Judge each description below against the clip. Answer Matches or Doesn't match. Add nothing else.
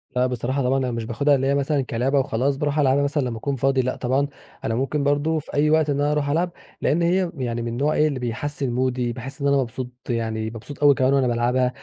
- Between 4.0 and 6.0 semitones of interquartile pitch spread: Doesn't match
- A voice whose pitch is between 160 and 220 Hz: Doesn't match